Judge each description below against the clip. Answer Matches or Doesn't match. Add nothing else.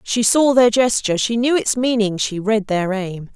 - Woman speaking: Matches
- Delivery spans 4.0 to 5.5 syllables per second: Matches